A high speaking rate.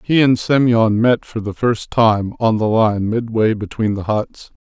No: average, 195 wpm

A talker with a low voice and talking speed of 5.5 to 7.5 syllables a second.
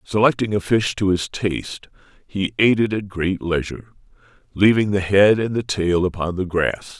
No: low, 100 Hz; 4.9 syllables/s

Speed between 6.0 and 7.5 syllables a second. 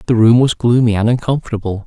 Yes: 6.5 syllables/s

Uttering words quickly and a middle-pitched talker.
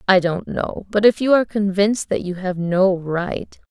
No: fast, 210 wpm; high, 195 Hz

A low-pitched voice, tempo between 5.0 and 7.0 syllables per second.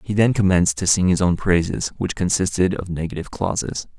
Yes: very low, 90 Hz; 5.9 syllables/s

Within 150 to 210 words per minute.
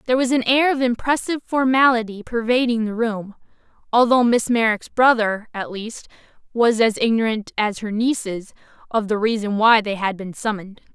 Yes: average, 165 wpm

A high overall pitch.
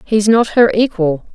Yes: high, 210 Hz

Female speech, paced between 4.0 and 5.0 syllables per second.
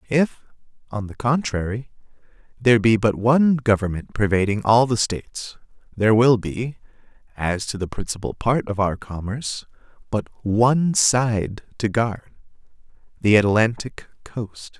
No: male; 4.4 syllables/s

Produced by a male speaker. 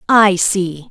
No: female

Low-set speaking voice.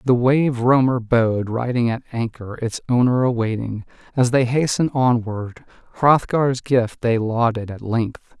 Yes: low, 120 Hz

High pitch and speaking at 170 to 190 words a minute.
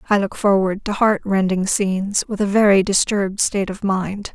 Yes: high, 200 Hz; average, 180 wpm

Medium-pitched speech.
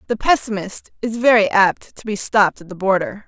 No: high, 210 Hz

